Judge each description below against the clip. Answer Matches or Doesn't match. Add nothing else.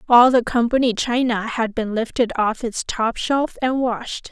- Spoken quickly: Doesn't match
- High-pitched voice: Matches